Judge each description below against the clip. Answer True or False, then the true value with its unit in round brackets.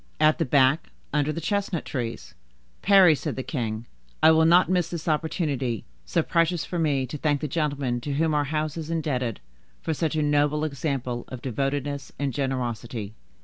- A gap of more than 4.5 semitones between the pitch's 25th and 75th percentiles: False (3.4 semitones)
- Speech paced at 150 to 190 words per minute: True (180 wpm)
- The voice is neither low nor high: True (145 Hz)